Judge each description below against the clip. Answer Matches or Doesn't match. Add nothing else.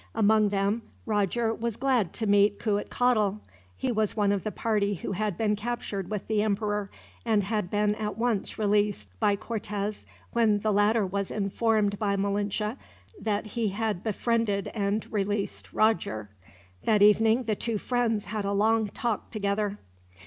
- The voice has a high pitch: Matches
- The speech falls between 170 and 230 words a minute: Doesn't match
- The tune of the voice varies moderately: Doesn't match